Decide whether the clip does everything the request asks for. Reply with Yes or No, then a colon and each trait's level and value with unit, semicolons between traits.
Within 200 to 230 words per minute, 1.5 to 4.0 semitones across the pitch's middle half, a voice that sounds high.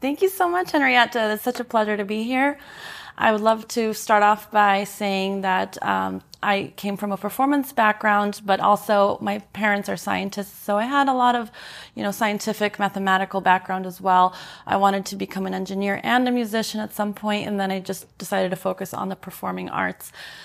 Yes: fast, 205 wpm; narrow, 2.4 semitones; high, 205 Hz